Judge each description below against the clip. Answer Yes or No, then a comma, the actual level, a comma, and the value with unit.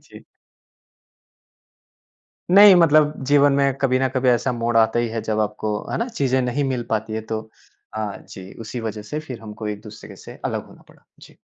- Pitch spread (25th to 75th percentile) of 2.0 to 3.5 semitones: No, average, 4.1 semitones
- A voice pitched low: Yes, low, 120 Hz